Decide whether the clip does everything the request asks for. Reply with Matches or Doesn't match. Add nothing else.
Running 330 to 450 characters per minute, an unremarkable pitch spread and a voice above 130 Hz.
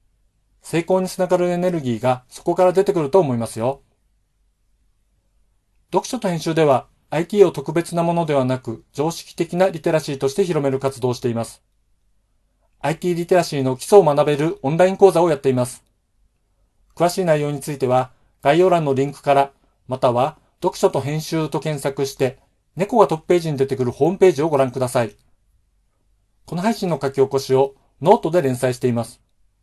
Doesn't match